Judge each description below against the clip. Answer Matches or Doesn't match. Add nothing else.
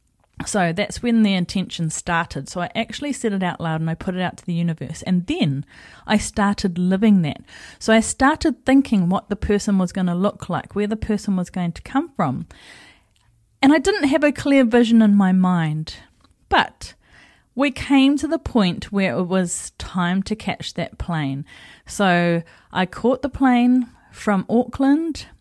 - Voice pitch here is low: Doesn't match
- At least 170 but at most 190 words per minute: Matches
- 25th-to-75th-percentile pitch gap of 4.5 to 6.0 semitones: Matches